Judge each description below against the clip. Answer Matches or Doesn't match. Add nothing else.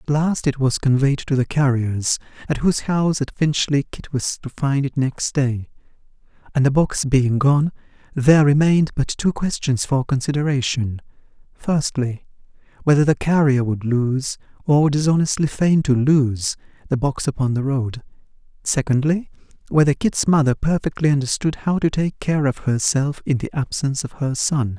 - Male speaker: Matches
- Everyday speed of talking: Matches